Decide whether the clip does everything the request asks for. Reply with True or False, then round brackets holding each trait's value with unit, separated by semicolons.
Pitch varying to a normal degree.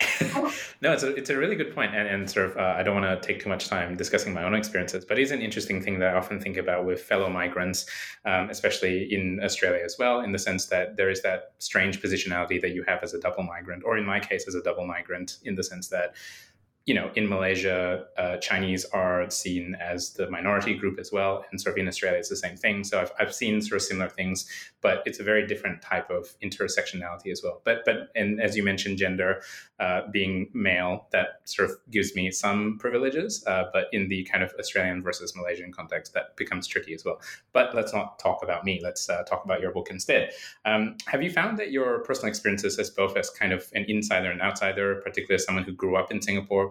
False (1.9 semitones)